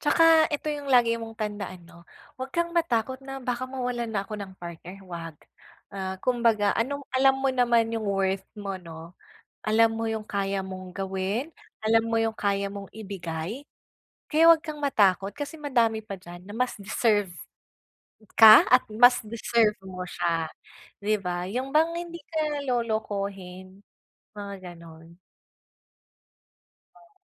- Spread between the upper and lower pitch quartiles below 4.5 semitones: No, average, 4.8 semitones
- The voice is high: Yes, high, 220 Hz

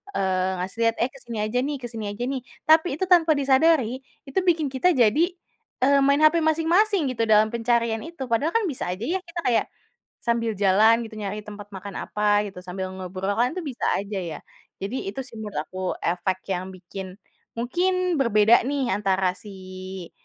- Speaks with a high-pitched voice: Yes, high, 230 Hz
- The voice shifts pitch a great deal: Yes, wide, 6.5 semitones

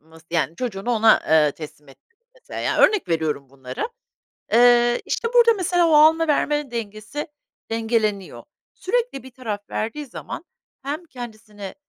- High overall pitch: Yes, high, 230 Hz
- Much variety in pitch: Yes, wide, 7.5 semitones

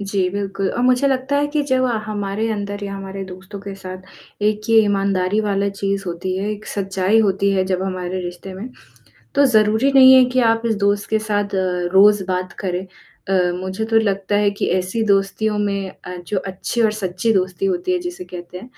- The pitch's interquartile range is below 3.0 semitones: Yes, narrow, 2.6 semitones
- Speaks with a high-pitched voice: Yes, high, 200 Hz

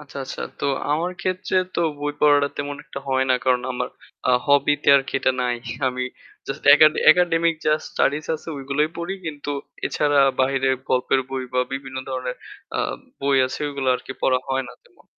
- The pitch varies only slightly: Yes, narrow, 2.3 semitones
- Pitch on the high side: No, medium, 140 Hz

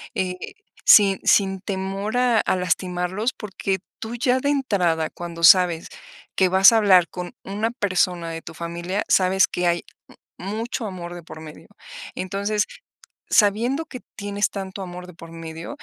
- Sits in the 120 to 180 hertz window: No, high, 190 Hz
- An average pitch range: Yes, average, 3.0 semitones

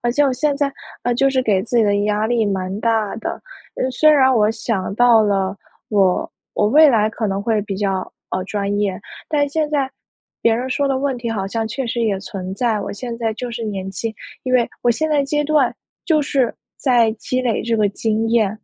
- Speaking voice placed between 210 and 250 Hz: Yes, high, 230 Hz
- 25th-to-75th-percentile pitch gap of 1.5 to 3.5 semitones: No, average, 3.9 semitones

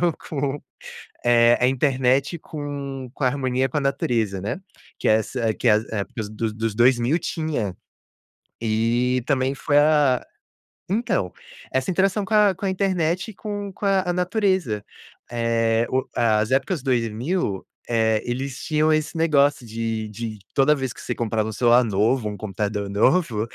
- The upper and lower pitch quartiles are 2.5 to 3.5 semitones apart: No, wide, 5.5 semitones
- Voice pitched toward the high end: No, low, 130 Hz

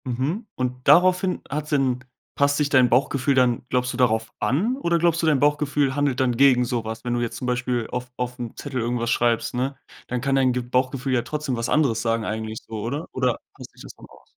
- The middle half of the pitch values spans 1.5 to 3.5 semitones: Yes, average, 2.9 semitones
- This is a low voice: Yes, low, 125 Hz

